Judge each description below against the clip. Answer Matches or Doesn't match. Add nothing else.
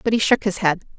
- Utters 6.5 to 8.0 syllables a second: Matches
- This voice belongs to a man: Doesn't match